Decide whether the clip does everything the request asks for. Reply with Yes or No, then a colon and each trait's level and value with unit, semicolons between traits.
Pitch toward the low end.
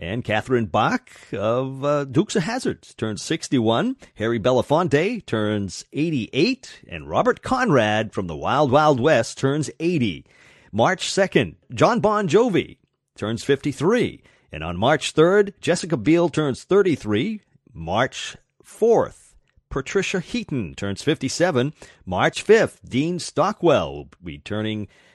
No: medium, 145 Hz